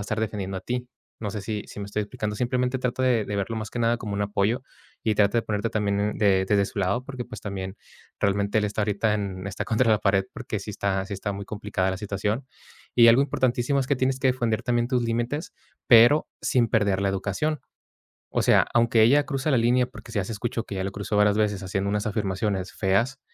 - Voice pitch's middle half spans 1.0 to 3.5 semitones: Yes, average, 3.2 semitones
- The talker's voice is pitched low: Yes, low, 105 Hz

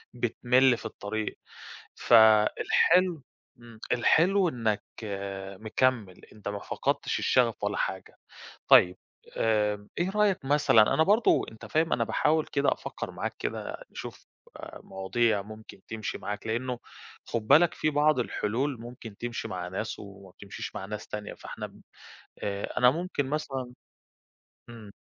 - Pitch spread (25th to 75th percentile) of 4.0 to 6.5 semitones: Yes, average, 5.3 semitones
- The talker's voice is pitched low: Yes, low, 115 Hz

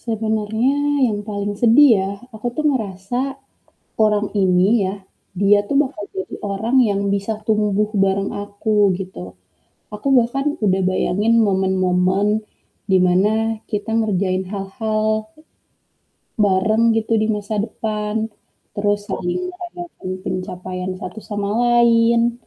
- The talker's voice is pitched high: Yes, high, 210 Hz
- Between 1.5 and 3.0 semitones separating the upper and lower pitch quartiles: Yes, average, 2.7 semitones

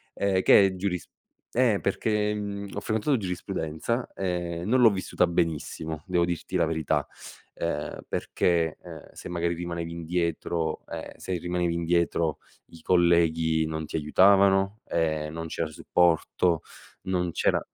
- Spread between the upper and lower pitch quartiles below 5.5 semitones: Yes, average, 2.9 semitones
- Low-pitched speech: Yes, very low, 85 Hz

